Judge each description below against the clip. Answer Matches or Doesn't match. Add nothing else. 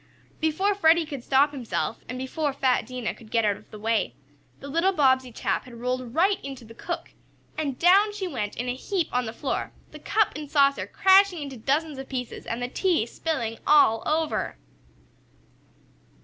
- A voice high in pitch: Matches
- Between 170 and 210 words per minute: Matches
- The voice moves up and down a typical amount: Matches